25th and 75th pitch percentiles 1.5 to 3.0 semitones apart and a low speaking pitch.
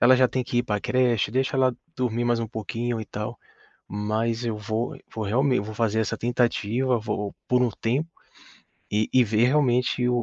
Yes: narrow, 2.5 semitones; low, 120 Hz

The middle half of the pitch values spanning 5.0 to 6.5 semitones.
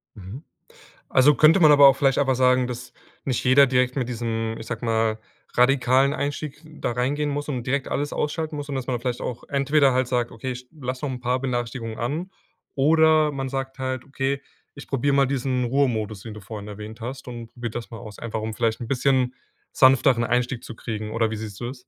No: average, 3.0 semitones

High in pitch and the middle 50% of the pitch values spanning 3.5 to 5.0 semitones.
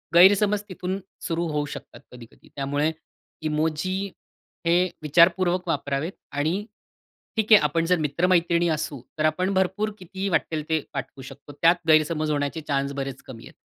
No: medium, 165 Hz; average, 3.9 semitones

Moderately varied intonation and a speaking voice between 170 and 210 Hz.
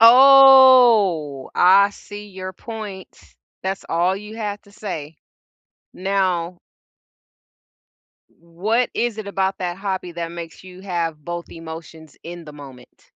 Yes: average, 3.7 semitones; medium, 185 Hz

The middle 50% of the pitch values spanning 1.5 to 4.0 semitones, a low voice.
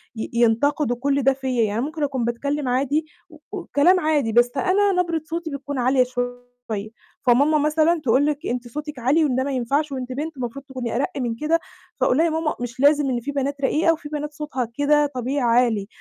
No: average, 3.4 semitones; very high, 280 Hz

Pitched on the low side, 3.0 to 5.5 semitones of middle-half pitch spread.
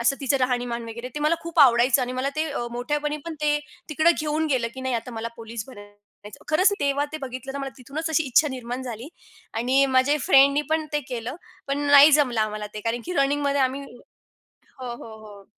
No: very high, 260 Hz; average, 3.6 semitones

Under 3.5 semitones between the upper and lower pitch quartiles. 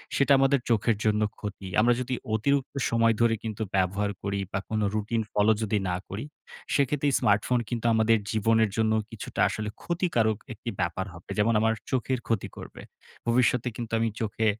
Yes: narrow, 2.5 semitones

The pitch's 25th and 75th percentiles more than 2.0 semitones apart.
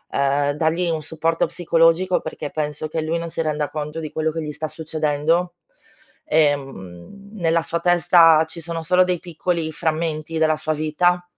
No: narrow, 1.7 semitones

